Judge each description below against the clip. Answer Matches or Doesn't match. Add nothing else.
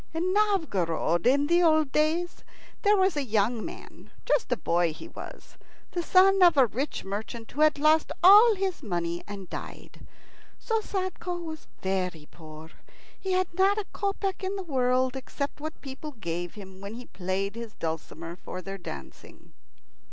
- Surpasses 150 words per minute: Matches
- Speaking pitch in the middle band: Doesn't match